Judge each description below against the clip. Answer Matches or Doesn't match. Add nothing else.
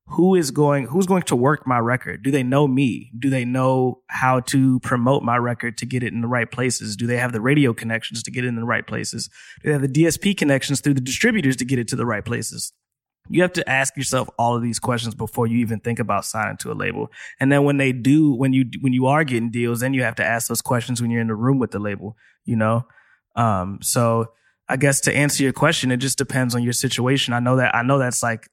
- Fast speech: Matches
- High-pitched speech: Doesn't match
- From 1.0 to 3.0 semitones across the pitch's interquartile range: Matches